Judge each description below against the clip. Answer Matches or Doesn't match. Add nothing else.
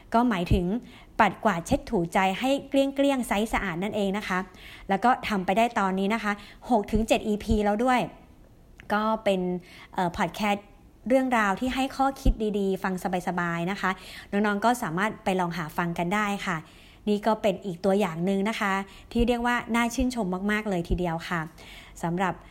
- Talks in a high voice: Matches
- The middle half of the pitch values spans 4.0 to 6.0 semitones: Doesn't match